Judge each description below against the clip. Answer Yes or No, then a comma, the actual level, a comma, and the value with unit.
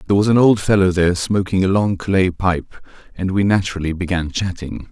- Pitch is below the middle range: Yes, very low, 95 Hz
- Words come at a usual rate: Yes, average, 195 wpm